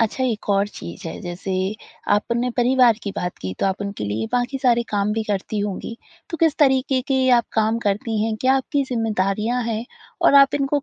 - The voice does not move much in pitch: No, average, 4.3 semitones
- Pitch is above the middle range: Yes, high, 225 Hz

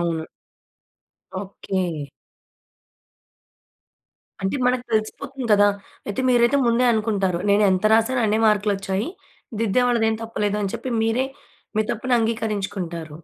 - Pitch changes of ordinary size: Yes, average, 3.3 semitones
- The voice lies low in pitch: No, high, 215 Hz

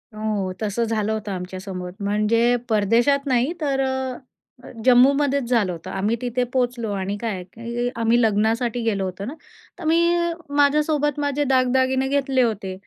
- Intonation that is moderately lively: Yes, average, 4.1 semitones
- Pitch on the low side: No, high, 235 Hz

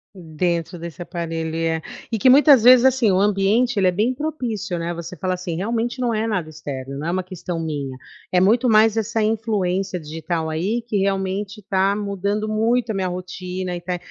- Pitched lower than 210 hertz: Yes, high, 190 Hz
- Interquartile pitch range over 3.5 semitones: Yes, average, 4.3 semitones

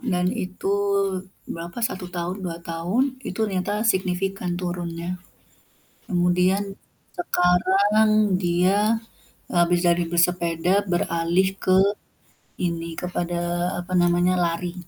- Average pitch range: No, narrow, 1.7 semitones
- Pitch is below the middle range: No, medium, 180 Hz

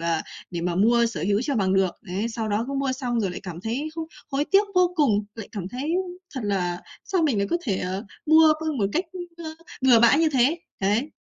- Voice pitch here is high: Yes, high, 235 Hz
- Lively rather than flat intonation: Yes, wide, 7.4 semitones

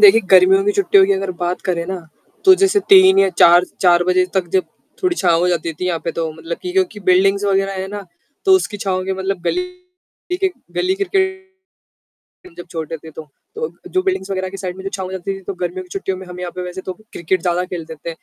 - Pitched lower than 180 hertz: No, high, 190 Hz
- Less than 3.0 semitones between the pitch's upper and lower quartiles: Yes, narrow, 2.6 semitones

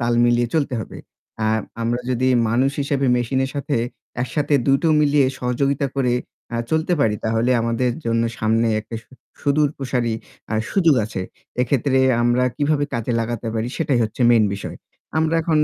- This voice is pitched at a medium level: No, low, 125 Hz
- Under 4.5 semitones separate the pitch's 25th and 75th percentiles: Yes, average, 3.4 semitones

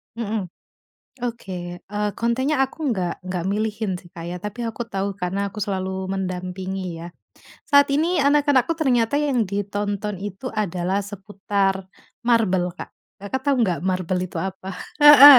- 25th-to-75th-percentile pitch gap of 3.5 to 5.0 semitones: Yes, average, 4.4 semitones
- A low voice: No, high, 205 Hz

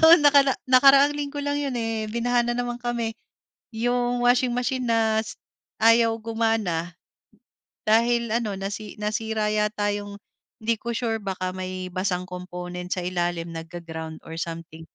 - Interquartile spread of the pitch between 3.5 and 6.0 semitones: Yes, average, 4.8 semitones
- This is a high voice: Yes, high, 220 Hz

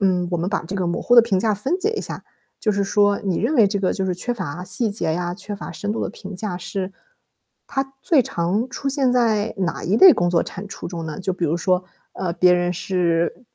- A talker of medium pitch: No, high, 195 Hz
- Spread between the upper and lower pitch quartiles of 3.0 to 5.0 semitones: Yes, average, 3.5 semitones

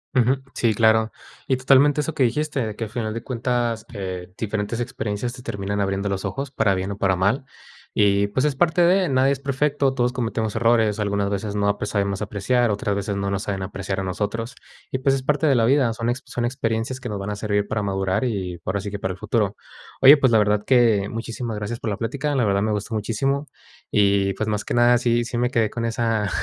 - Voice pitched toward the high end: No, low, 110 Hz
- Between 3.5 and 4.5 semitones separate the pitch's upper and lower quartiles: Yes, average, 3.8 semitones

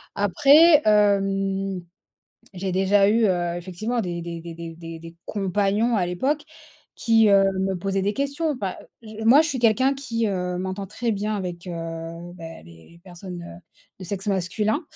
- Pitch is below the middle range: No, high, 195 Hz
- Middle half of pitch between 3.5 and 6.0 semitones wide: Yes, average, 4.0 semitones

